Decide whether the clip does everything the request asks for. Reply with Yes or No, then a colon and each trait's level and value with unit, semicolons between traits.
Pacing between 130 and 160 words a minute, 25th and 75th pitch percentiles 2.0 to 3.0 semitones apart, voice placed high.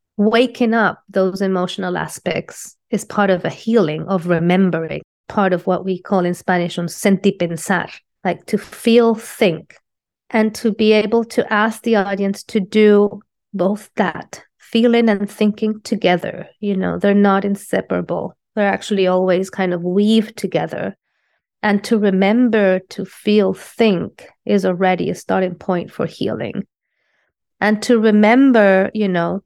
Yes: average, 145 wpm; average, 2.7 semitones; high, 200 Hz